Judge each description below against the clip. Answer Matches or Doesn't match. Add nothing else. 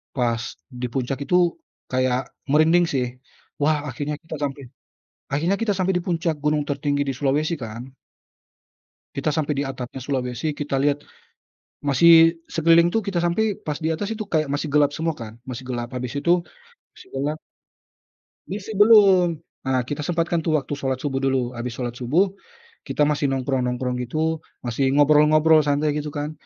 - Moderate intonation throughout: Matches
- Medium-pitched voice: Matches